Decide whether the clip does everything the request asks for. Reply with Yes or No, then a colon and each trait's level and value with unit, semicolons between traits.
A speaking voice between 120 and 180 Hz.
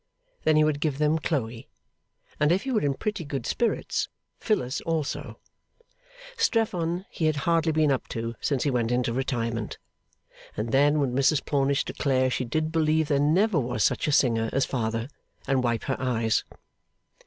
Yes: medium, 140 Hz